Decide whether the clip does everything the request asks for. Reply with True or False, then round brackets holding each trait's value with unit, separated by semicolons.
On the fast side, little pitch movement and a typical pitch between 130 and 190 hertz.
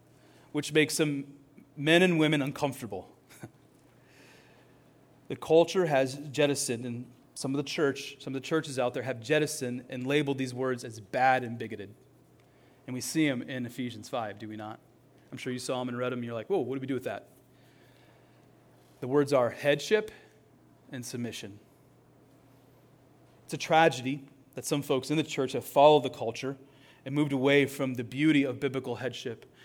False (180 wpm; 2.1 semitones; 135 Hz)